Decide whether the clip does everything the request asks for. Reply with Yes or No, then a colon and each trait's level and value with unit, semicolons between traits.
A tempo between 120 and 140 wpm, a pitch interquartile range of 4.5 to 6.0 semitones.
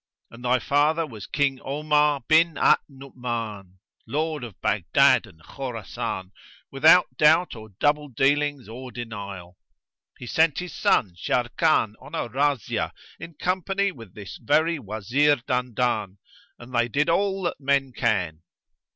Yes: slow, 135 wpm; average, 4.8 semitones